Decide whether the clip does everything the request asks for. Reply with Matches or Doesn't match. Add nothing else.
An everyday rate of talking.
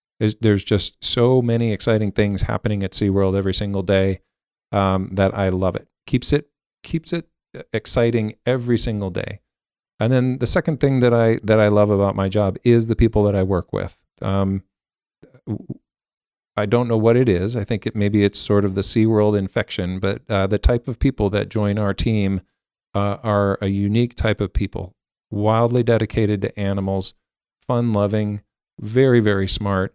Matches